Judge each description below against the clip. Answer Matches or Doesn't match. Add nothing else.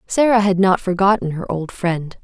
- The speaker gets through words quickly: Doesn't match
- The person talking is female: Matches